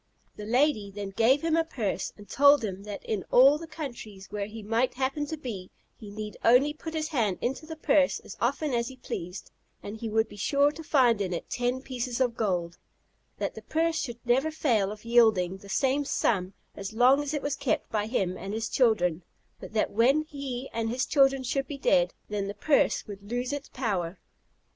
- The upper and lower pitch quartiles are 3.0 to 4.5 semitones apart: No, average, 5.2 semitones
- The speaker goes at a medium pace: No, fast, 210 wpm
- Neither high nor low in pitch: No, high, 240 Hz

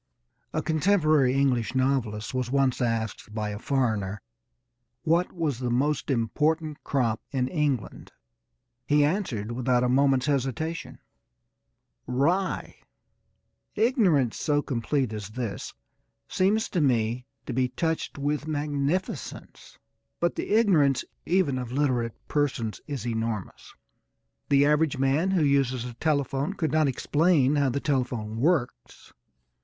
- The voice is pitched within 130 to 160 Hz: Yes, low, 135 Hz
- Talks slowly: Yes, slow, 125 wpm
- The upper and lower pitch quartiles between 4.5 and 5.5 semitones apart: No, average, 3.9 semitones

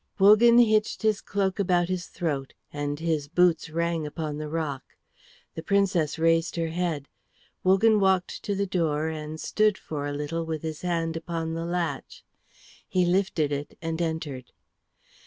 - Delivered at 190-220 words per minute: No, average, 155 wpm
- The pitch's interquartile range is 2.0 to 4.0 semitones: Yes, average, 3.1 semitones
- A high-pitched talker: No, medium, 165 Hz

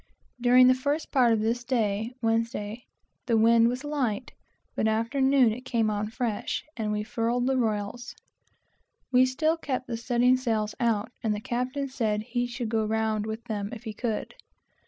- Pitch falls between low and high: No, high, 235 Hz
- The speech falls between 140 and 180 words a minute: Yes, average, 175 wpm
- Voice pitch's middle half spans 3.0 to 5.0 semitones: No, narrow, 2.6 semitones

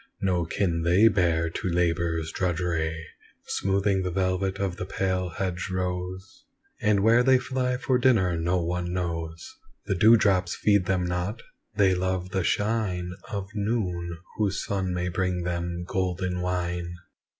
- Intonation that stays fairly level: Yes, narrow, 2.1 semitones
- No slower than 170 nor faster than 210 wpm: No, average, 150 wpm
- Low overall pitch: Yes, very low, 90 Hz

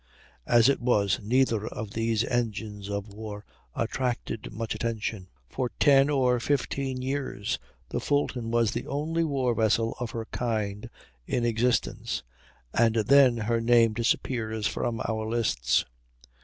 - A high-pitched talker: No, low, 115 Hz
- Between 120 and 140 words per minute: Yes, slow, 135 wpm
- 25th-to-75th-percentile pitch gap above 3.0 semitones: No, narrow, 2.5 semitones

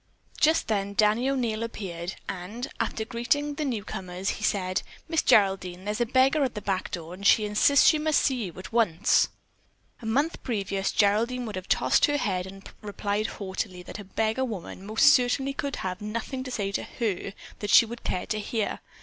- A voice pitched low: No, high, 215 Hz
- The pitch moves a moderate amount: Yes, average, 4.2 semitones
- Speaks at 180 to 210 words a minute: Yes, average, 200 wpm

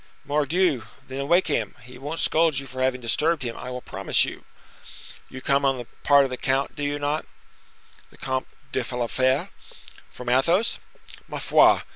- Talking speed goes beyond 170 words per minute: Yes, average, 180 wpm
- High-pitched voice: No, low, 135 Hz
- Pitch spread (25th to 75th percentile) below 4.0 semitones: Yes, narrow, 2.5 semitones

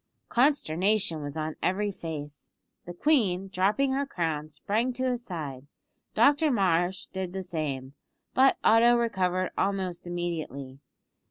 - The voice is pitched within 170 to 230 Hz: Yes, medium, 185 Hz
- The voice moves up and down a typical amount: No, wide, 6.1 semitones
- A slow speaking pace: Yes, slow, 125 wpm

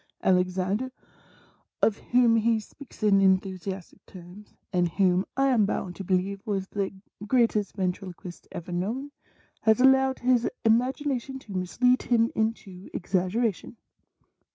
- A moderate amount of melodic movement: Yes, average, 4.5 semitones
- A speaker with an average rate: No, slow, 130 wpm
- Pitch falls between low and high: No, high, 205 Hz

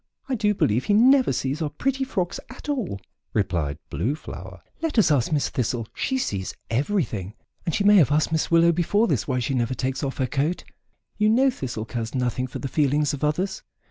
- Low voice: No, medium, 150 Hz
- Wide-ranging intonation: Yes, wide, 8.5 semitones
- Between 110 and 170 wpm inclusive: No, fast, 205 wpm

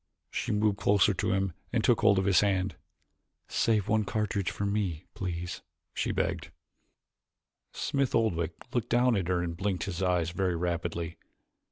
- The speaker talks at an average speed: Yes, average, 160 wpm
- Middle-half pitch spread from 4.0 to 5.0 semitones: No, average, 3.0 semitones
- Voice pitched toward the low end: Yes, very low, 95 Hz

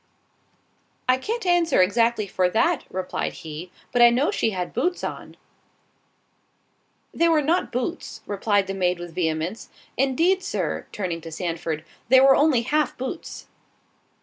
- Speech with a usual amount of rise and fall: No, wide, 8.7 semitones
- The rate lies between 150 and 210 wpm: No, average, 140 wpm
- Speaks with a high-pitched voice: Yes, high, 230 Hz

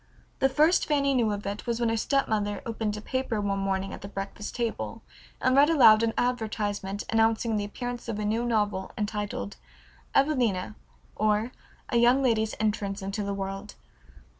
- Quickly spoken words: No, average, 170 wpm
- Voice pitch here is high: Yes, high, 215 Hz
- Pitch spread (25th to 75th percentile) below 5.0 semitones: Yes, average, 2.9 semitones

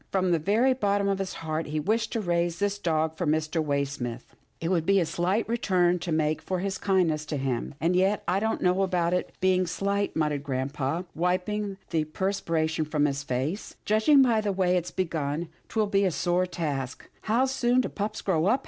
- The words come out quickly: Yes, fast, 215 wpm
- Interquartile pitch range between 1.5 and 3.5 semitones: No, average, 4.2 semitones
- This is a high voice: No, medium, 180 Hz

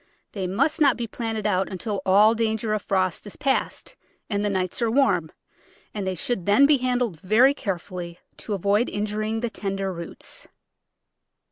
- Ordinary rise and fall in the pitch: Yes, average, 3.6 semitones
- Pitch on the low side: No, high, 210 Hz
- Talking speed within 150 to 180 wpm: Yes, average, 165 wpm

